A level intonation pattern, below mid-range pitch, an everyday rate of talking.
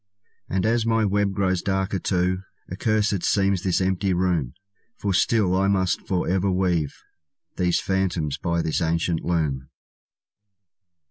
No: narrow, 2.1 semitones; very low, 95 Hz; slow, 130 wpm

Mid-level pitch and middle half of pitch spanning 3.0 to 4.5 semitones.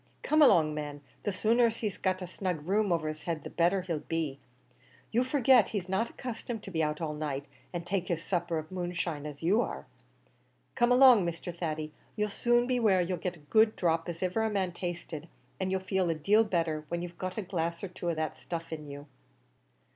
Yes: medium, 175 Hz; average, 4.0 semitones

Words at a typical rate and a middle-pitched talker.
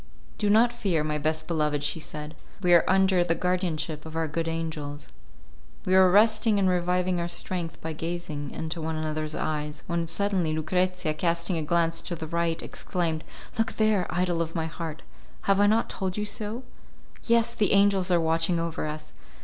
Yes: average, 180 wpm; medium, 170 Hz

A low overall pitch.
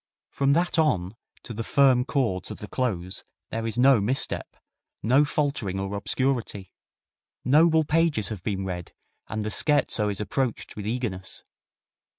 Yes: low, 115 Hz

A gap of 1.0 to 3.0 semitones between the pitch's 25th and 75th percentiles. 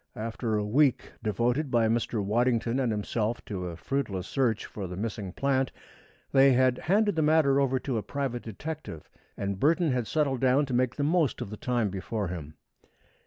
No: average, 4.5 semitones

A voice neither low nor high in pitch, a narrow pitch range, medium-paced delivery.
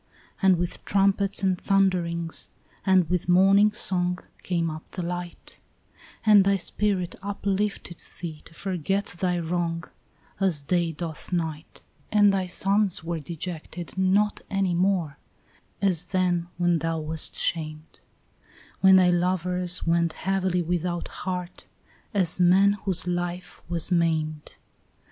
No: medium, 180 Hz; narrow, 2.2 semitones; slow, 125 wpm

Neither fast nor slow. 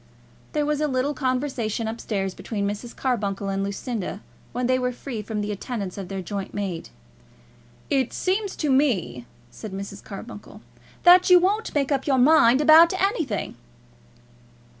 Yes: average, 160 wpm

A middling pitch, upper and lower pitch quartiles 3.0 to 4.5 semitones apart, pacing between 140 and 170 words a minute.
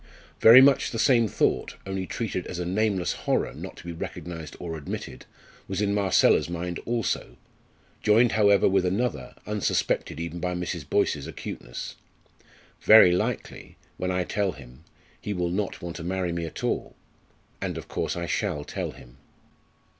No: very low, 90 Hz; average, 3.3 semitones; average, 160 wpm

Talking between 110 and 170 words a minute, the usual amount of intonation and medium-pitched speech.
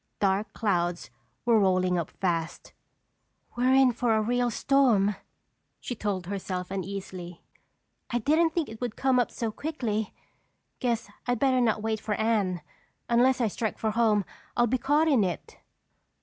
No: average, 155 wpm; average, 4.0 semitones; high, 220 Hz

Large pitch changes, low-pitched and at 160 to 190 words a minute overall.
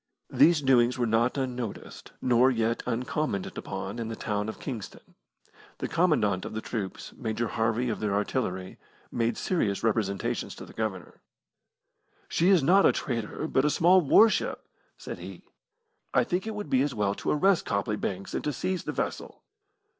Yes: wide, 5.7 semitones; low, 120 Hz; average, 170 wpm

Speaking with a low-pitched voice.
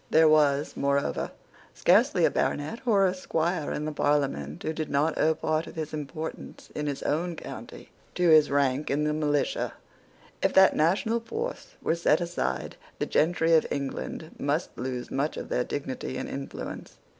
No: medium, 155 Hz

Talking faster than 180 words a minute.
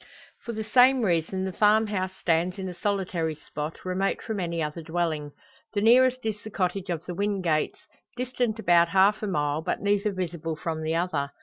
Yes: average, 190 wpm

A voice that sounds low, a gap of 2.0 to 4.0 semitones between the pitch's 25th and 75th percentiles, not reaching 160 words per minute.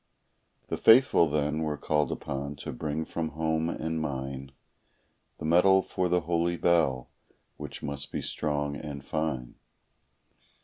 Yes: very low, 75 Hz; narrow, 2.6 semitones; slow, 135 wpm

